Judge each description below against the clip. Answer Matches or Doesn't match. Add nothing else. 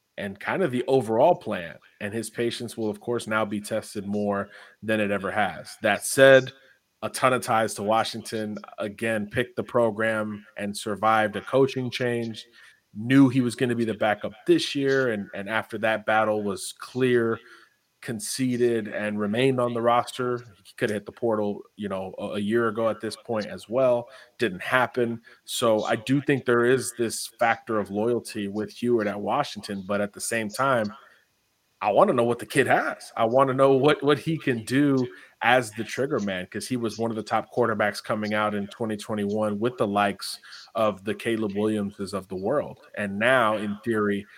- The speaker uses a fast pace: Doesn't match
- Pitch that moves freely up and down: Doesn't match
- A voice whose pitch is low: Matches